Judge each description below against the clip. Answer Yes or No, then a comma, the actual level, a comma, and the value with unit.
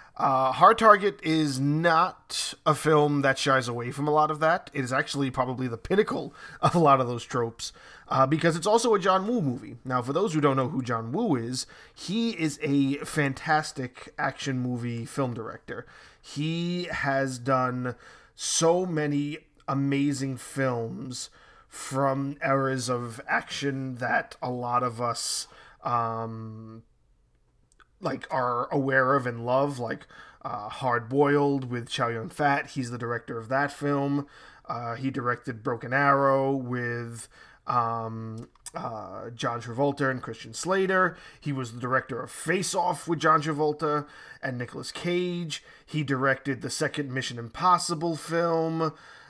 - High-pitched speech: No, low, 135 Hz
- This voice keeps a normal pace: Yes, average, 150 wpm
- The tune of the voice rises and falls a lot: No, average, 3.7 semitones